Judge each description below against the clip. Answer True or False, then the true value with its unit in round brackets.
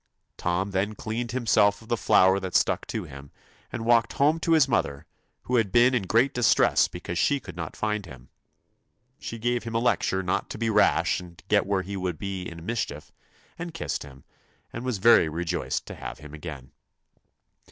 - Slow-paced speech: False (195 wpm)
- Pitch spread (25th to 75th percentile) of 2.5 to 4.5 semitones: False (5.2 semitones)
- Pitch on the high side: False (100 Hz)